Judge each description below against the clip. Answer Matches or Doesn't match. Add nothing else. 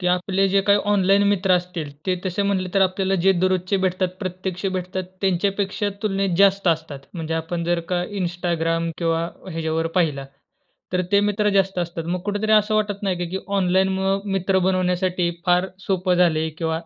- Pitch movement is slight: Matches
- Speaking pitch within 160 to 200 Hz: Matches